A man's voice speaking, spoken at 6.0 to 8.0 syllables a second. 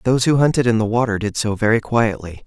Yes: male; 6.4 syllables/s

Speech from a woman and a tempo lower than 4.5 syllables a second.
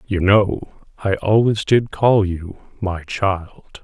No: male; 3.1 syllables/s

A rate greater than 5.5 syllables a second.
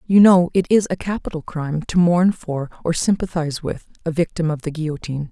Yes: 5.9 syllables/s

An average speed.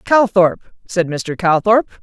No: slow, 120 wpm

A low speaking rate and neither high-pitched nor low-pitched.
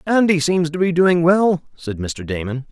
No: average, 200 wpm; medium, 160 Hz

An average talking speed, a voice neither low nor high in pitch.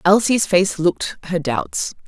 Yes: average, 145 wpm; medium, 180 Hz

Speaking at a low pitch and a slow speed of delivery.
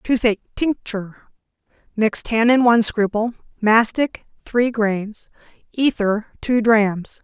No: high, 225 Hz; slow, 90 wpm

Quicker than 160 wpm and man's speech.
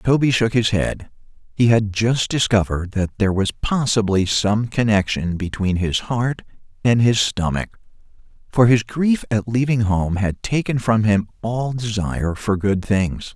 No: average, 155 wpm; male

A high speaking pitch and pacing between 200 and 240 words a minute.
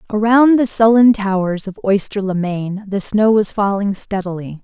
No: high, 205 Hz; average, 170 wpm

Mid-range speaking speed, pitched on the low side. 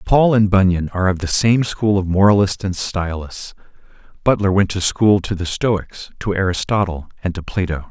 Yes: average, 180 wpm; very low, 95 Hz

